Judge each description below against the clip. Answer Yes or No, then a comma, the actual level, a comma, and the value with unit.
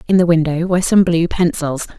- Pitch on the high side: No, medium, 170 Hz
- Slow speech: No, fast, 210 wpm